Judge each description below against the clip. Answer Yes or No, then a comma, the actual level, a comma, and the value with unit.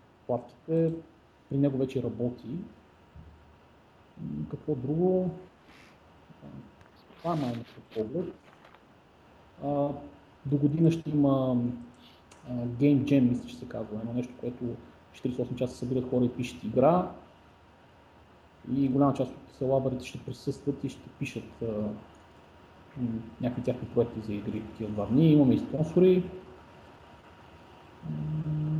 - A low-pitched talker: Yes, low, 125 Hz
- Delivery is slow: Yes, slow, 110 wpm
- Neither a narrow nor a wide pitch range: Yes, average, 3.8 semitones